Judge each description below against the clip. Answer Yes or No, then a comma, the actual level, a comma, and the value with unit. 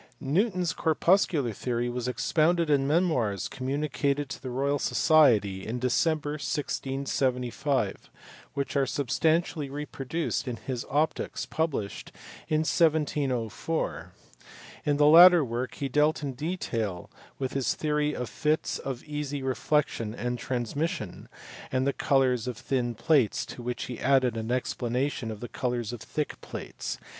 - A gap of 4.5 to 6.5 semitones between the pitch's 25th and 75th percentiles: No, average, 3.6 semitones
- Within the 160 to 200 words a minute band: No, average, 140 wpm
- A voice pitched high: No, low, 135 Hz